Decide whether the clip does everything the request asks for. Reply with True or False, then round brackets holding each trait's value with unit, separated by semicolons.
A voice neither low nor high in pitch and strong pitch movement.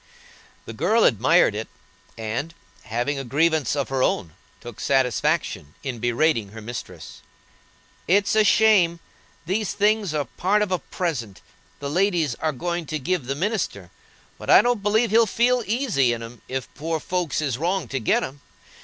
True (155 Hz; 8.0 semitones)